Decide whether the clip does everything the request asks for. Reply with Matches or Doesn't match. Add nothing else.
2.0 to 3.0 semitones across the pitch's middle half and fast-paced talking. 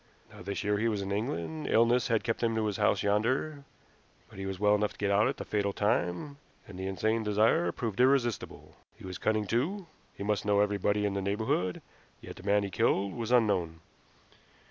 Matches